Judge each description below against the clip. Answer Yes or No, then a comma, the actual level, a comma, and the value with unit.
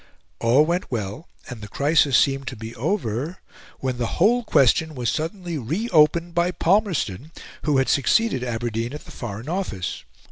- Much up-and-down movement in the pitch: Yes, wide, 6.4 semitones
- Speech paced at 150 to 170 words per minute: Yes, average, 165 wpm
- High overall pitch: No, medium, 140 Hz